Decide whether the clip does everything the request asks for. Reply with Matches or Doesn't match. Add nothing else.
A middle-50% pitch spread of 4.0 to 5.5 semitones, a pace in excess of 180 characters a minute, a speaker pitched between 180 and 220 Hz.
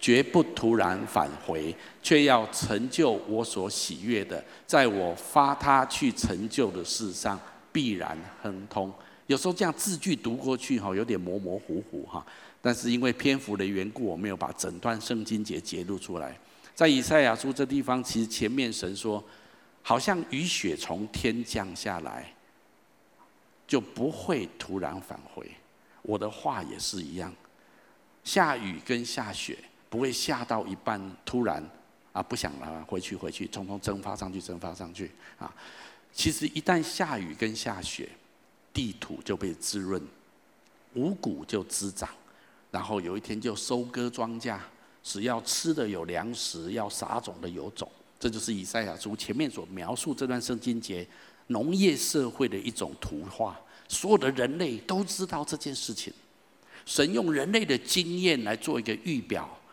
Doesn't match